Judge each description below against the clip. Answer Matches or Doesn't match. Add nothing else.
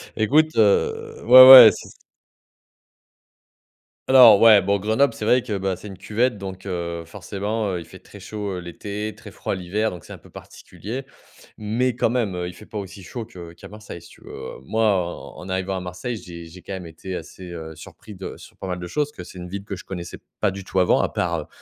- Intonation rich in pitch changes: Doesn't match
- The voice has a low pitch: Matches